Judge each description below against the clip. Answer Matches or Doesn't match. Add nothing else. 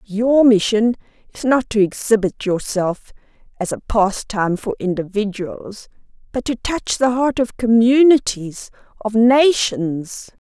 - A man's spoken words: Doesn't match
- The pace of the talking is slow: Matches